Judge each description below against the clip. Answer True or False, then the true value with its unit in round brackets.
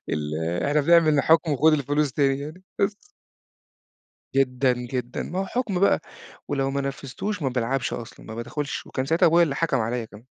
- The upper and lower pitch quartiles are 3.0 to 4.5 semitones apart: True (4.2 semitones)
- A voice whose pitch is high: False (140 Hz)